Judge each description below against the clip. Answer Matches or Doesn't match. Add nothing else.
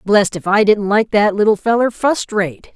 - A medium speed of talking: Doesn't match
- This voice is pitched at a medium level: Doesn't match